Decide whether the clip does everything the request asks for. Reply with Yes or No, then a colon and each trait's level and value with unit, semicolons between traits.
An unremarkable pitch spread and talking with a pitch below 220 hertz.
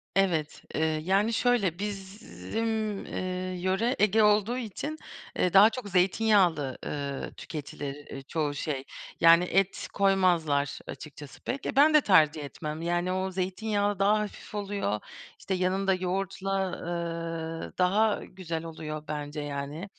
Yes: average, 4.3 semitones; medium, 185 Hz